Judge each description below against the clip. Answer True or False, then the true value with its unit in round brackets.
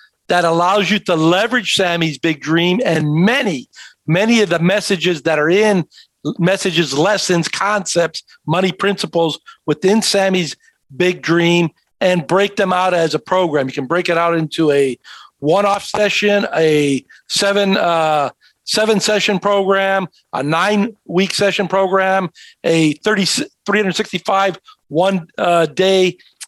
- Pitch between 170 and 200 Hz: True (185 Hz)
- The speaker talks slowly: True (130 wpm)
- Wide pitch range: False (3.4 semitones)